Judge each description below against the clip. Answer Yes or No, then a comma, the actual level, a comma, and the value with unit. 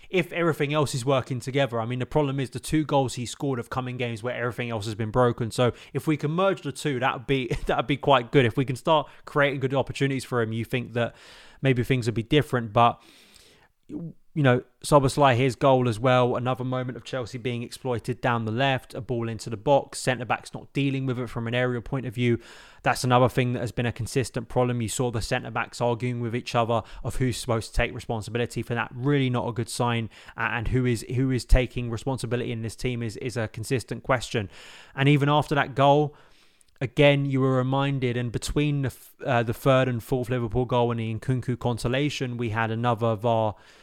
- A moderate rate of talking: No, fast, 220 wpm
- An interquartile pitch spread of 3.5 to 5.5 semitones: No, narrow, 2.4 semitones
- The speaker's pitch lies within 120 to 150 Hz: Yes, low, 125 Hz